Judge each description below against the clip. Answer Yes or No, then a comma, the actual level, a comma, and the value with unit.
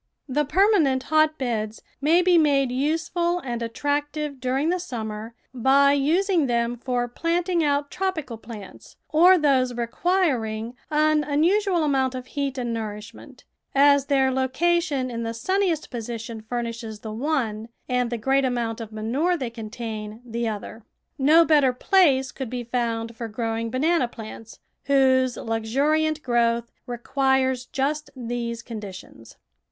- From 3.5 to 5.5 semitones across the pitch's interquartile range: Yes, average, 4.6 semitones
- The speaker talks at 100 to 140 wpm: Yes, slow, 135 wpm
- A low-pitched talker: No, very high, 260 Hz